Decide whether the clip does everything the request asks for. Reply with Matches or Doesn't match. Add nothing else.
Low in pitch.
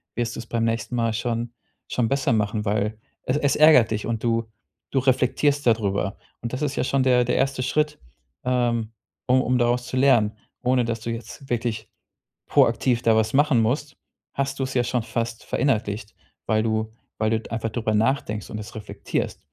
Matches